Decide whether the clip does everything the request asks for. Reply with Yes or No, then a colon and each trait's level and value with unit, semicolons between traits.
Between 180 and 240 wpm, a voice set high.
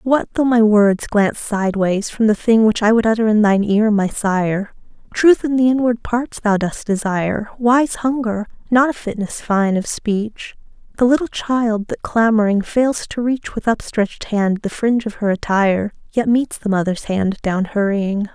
Yes: average, 185 wpm; high, 215 Hz